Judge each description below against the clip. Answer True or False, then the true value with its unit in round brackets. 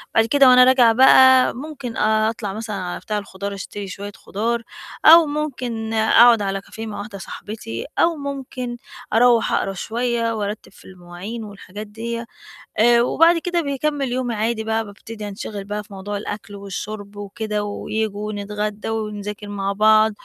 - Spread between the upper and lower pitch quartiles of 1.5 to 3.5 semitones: True (2.8 semitones)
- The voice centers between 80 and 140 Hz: False (220 Hz)